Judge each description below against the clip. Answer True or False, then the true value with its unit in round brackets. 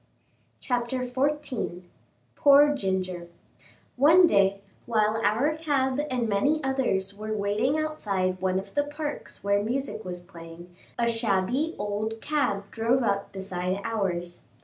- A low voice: False (220 Hz)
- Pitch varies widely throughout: True (5.9 semitones)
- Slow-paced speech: True (125 wpm)